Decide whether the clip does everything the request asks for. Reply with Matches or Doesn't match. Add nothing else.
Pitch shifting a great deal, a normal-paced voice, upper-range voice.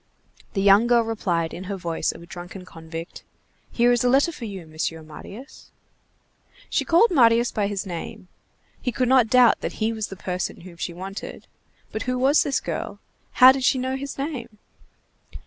Matches